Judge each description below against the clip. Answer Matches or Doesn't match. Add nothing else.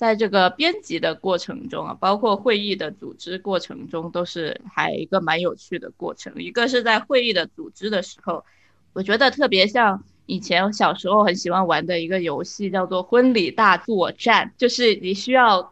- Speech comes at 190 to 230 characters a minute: Doesn't match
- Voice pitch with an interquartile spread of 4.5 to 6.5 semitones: Matches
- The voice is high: Matches